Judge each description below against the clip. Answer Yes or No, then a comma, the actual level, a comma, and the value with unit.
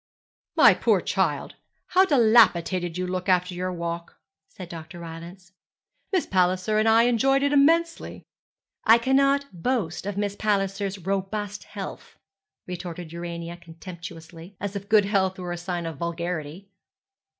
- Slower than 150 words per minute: Yes, average, 140 wpm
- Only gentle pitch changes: No, average, 3.8 semitones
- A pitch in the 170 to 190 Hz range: Yes, medium, 185 Hz